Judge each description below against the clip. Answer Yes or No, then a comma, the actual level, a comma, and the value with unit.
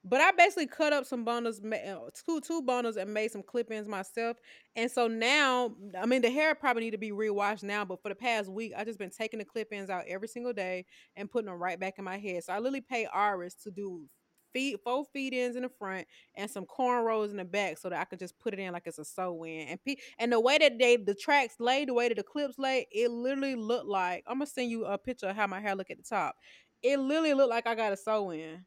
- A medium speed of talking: No, fast, 255 wpm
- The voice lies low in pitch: No, high, 225 Hz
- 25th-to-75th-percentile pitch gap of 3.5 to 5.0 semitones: Yes, average, 4.3 semitones